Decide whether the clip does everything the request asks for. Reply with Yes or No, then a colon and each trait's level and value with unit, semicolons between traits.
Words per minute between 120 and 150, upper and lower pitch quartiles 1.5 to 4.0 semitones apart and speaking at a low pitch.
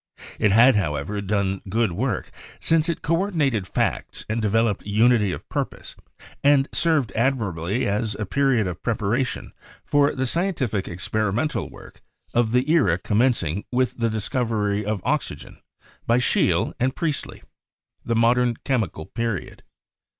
No: average, 145 wpm; average, 4.4 semitones; low, 115 Hz